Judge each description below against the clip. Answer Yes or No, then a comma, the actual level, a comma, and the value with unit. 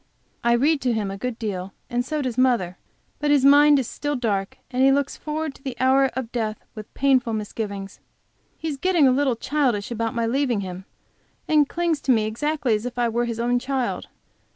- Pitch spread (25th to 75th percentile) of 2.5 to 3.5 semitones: No, average, 4.0 semitones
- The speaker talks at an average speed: No, fast, 210 wpm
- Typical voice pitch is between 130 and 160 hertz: No, very high, 250 Hz